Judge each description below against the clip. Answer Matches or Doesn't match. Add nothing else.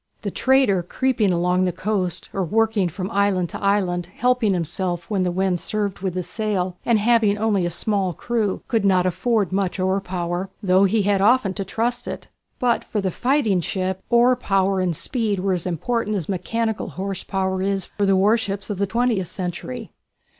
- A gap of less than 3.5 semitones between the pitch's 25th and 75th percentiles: Matches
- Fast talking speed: Doesn't match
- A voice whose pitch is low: Doesn't match